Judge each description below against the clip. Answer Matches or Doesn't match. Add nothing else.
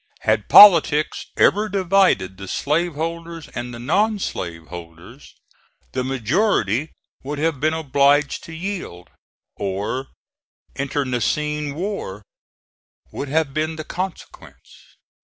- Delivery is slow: Matches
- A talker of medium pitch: Matches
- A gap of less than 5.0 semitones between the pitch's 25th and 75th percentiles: Doesn't match